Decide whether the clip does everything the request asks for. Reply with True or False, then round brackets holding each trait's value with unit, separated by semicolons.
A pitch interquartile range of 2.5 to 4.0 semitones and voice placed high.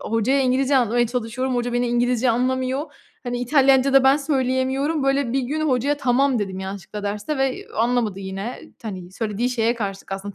True (3.2 semitones; 245 Hz)